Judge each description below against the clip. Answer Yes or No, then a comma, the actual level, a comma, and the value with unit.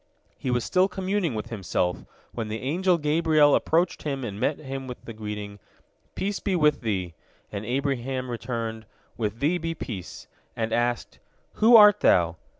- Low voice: Yes, low, 130 Hz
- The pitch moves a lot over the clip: Yes, wide, 6.8 semitones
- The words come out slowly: No, average, 165 wpm